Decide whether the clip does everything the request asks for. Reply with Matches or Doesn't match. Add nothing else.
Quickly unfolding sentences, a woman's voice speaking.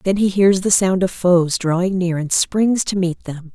Matches